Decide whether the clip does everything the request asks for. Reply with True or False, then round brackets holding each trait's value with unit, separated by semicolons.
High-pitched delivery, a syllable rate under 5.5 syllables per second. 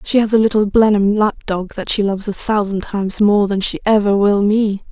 True (205 Hz; 5.3 syllables/s)